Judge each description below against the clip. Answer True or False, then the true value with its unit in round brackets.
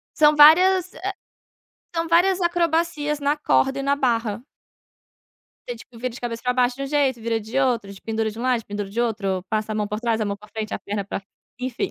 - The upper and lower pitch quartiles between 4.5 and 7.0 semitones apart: True (5.3 semitones)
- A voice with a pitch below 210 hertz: False (245 Hz)